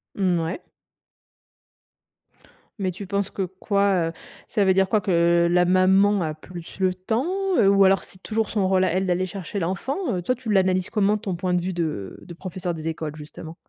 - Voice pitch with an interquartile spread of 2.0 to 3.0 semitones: Yes, narrow, 2.4 semitones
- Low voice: No, medium, 185 Hz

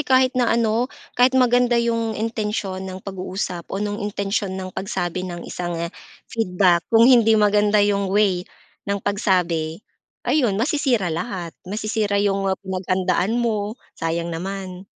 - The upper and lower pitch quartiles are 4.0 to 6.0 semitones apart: No, average, 3.5 semitones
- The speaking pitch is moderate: No, high, 200 Hz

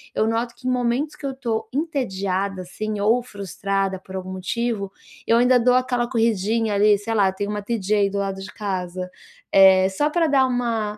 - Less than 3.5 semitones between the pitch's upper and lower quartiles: No, average, 3.8 semitones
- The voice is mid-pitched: No, high, 215 Hz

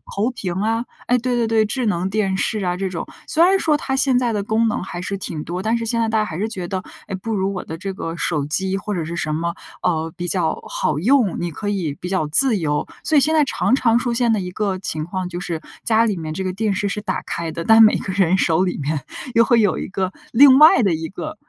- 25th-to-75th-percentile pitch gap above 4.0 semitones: Yes, average, 4.5 semitones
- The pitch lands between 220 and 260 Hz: No, high, 195 Hz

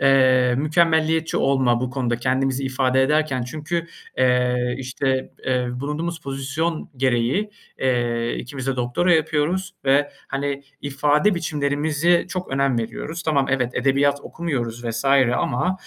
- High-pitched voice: No, low, 135 Hz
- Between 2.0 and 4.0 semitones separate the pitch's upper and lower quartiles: Yes, average, 3.5 semitones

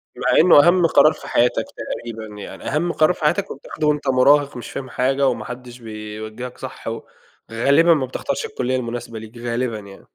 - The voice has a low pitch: Yes, low, 130 Hz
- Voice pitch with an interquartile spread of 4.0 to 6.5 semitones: Yes, average, 4.3 semitones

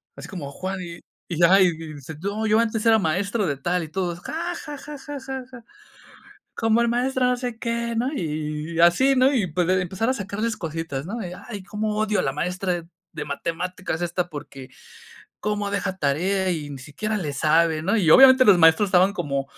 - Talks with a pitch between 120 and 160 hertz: No, high, 190 Hz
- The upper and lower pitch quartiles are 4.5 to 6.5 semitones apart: Yes, wide, 5.5 semitones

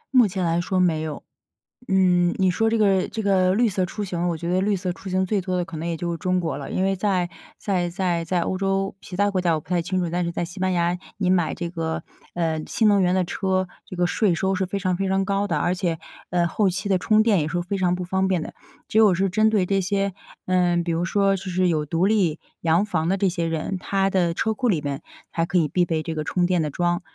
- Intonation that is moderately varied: No, narrow, 2.1 semitones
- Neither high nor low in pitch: Yes, medium, 180 Hz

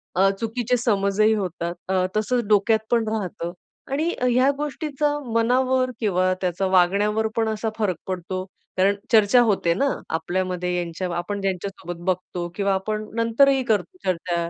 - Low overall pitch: No, high, 205 Hz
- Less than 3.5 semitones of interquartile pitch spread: No, average, 4.1 semitones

